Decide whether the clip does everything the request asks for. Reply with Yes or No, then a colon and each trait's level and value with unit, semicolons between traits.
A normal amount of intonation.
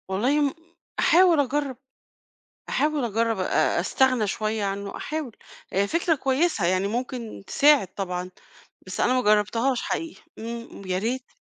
No: wide, 5.7 semitones